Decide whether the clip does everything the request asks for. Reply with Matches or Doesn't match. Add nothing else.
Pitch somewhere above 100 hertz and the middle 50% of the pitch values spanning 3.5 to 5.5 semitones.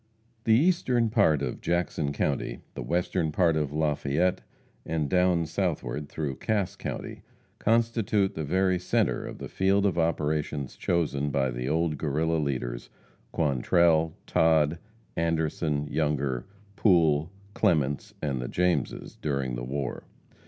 Doesn't match